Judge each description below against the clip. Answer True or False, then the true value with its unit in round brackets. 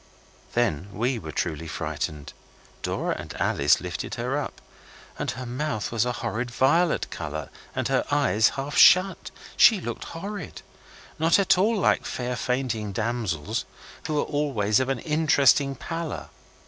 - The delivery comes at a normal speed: True (150 wpm)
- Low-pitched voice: True (125 Hz)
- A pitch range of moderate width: False (6.0 semitones)